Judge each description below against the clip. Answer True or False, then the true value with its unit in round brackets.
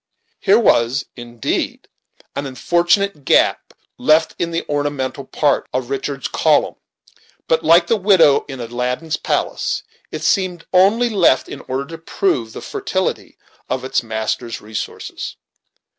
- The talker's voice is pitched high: False (145 Hz)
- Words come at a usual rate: False (130 wpm)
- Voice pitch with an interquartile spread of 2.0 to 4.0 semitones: False (5.2 semitones)